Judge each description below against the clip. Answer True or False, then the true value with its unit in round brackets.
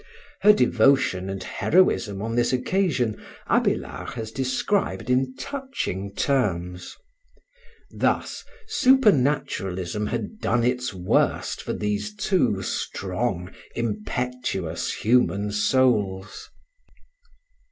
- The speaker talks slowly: True (90 wpm)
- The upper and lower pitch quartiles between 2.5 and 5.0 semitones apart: False (5.4 semitones)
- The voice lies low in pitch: True (120 Hz)